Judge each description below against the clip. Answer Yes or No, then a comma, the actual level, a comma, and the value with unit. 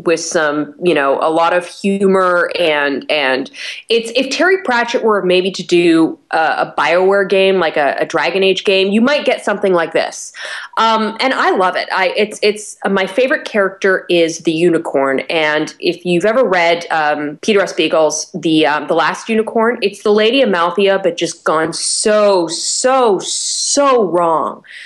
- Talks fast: No, average, 180 wpm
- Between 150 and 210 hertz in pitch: Yes, high, 190 Hz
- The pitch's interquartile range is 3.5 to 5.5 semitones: Yes, average, 5.1 semitones